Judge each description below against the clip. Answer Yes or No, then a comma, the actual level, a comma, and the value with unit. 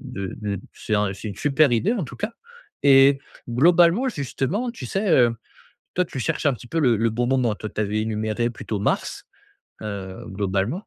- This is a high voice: No, low, 120 Hz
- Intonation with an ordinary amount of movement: No, wide, 6.5 semitones